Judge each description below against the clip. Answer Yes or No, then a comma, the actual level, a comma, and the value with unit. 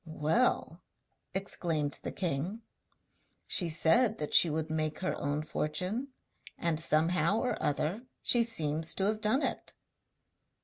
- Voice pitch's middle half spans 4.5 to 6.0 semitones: Yes, wide, 5.5 semitones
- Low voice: No, medium, 170 Hz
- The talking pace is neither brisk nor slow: No, slow, 130 wpm